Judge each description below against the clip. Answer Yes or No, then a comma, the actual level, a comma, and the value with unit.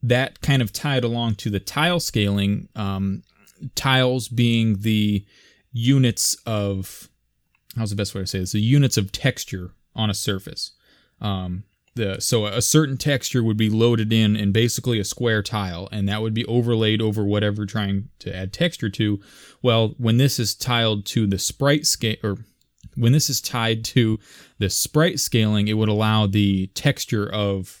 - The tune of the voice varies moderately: Yes, average, 3.1 semitones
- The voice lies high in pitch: No, low, 110 Hz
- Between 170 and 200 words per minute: Yes, average, 175 wpm